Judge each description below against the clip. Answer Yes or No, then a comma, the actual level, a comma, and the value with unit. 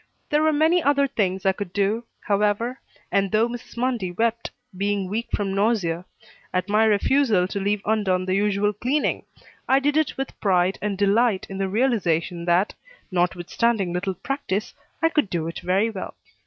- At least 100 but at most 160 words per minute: No, average, 170 wpm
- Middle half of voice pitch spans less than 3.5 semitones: No, average, 3.9 semitones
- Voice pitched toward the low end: No, high, 205 Hz